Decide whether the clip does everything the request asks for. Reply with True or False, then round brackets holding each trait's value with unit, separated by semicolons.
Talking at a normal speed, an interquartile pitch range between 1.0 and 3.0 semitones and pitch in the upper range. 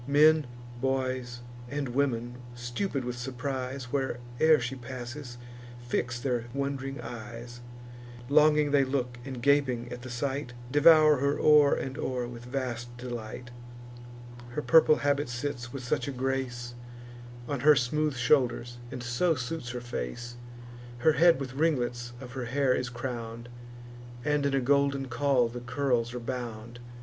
False (145 wpm; 2.7 semitones; 130 Hz)